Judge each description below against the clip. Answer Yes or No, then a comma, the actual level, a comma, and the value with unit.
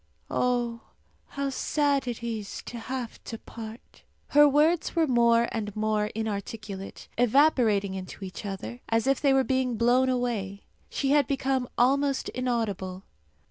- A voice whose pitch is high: Yes, high, 240 Hz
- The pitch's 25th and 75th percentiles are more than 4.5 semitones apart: No, average, 3.7 semitones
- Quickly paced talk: No, average, 140 wpm